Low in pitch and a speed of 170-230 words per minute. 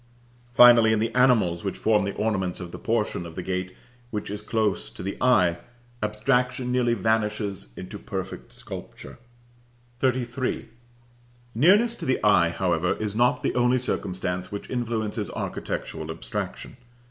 No: low, 105 Hz; average, 145 wpm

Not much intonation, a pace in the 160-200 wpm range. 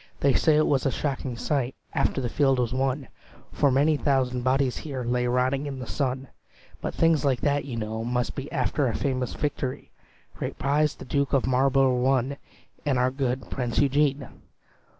Yes: narrow, 2.0 semitones; average, 185 wpm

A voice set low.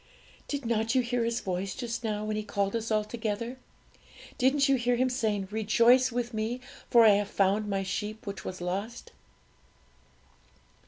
No: high, 220 Hz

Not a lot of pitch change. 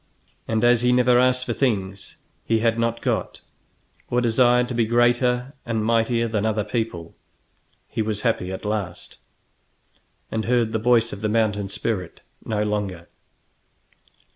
Yes: narrow, 2.3 semitones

